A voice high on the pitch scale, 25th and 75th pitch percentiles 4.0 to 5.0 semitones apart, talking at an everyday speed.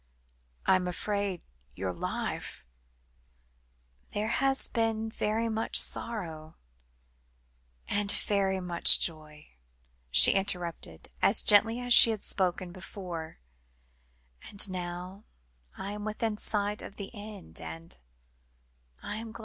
No: high, 195 Hz; average, 4.6 semitones; slow, 115 wpm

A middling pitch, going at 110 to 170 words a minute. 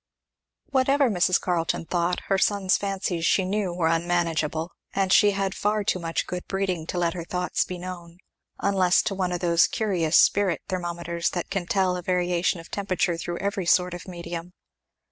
No: medium, 180 Hz; average, 180 wpm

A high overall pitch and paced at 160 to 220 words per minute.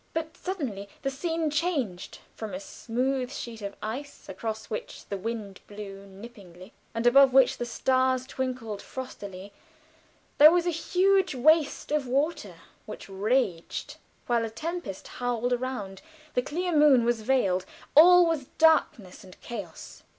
No: very high, 250 Hz; average, 145 wpm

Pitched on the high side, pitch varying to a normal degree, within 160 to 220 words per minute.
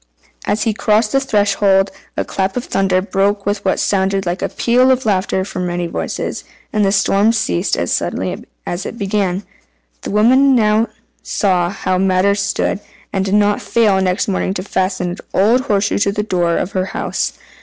No: high, 200 Hz; narrow, 2.0 semitones; average, 190 wpm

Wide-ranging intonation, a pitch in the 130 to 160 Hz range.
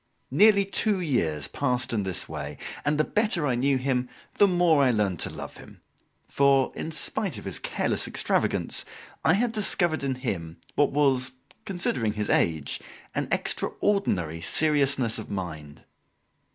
Yes: wide, 8.1 semitones; low, 135 Hz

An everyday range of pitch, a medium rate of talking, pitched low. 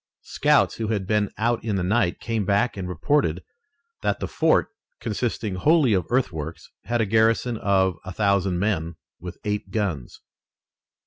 Yes: average, 3.6 semitones; average, 155 wpm; low, 100 Hz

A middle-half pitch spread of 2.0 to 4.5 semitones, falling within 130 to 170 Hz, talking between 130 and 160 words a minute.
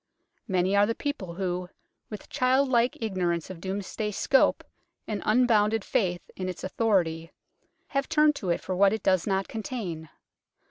No: average, 3.9 semitones; high, 200 Hz; average, 155 wpm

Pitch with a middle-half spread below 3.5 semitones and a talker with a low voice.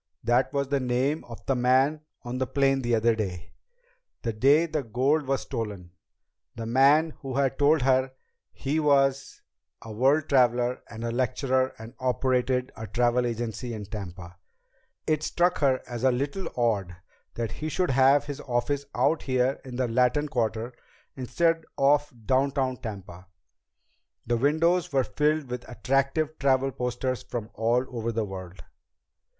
Yes: average, 3.0 semitones; low, 130 Hz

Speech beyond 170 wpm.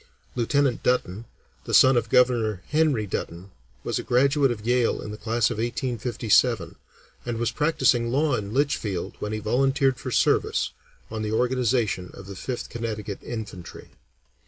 No: average, 155 wpm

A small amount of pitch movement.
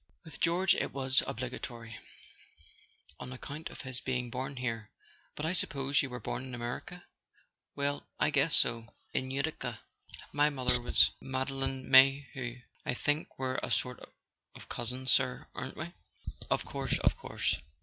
Yes: narrow, 2.3 semitones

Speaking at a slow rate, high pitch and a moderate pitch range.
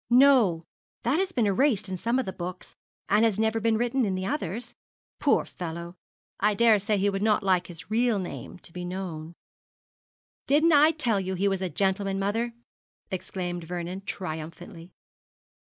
No: average, 170 wpm; high, 195 Hz; average, 4.2 semitones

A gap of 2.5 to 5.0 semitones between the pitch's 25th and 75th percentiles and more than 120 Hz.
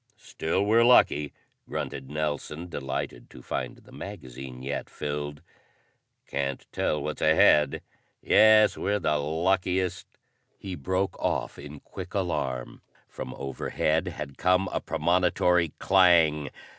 No: average, 4.2 semitones; very low, 80 Hz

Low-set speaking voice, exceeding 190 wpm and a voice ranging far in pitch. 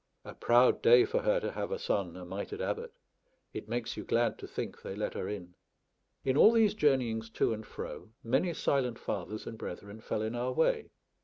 Yes: low, 120 Hz; fast, 205 wpm; wide, 5.8 semitones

